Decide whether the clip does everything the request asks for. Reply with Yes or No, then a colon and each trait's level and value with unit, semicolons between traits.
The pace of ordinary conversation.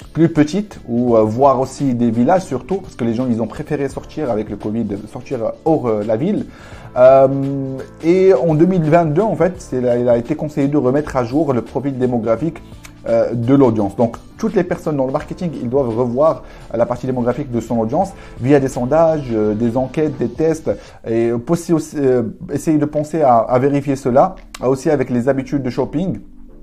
Yes: average, 195 wpm